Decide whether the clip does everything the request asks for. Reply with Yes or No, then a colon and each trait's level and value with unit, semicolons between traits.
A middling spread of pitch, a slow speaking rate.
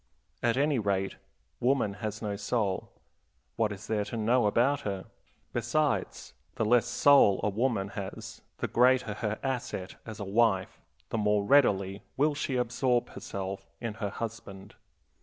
No: average, 3.5 semitones; average, 150 wpm